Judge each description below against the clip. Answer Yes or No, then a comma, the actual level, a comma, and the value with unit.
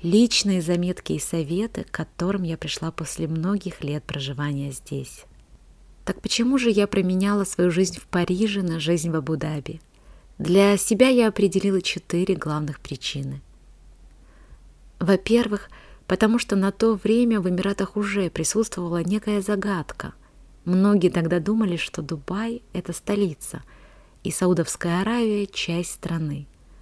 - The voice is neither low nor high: Yes, medium, 180 Hz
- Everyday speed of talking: Yes, average, 130 wpm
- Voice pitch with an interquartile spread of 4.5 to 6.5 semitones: No, average, 3.9 semitones